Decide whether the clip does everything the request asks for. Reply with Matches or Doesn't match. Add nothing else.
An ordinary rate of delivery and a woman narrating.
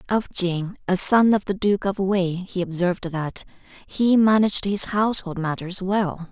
Matches